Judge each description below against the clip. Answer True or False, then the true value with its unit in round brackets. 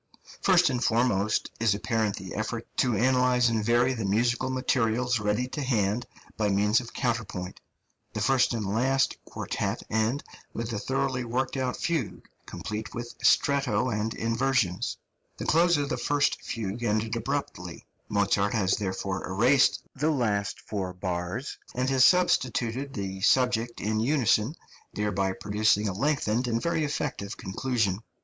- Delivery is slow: False (145 wpm)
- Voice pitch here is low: True (115 Hz)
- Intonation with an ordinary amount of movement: True (3.9 semitones)